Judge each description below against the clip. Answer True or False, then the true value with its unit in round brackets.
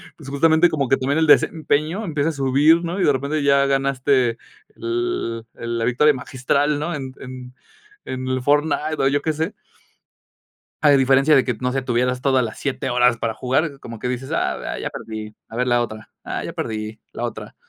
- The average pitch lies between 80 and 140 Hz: True (135 Hz)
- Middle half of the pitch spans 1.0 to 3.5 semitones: True (3.2 semitones)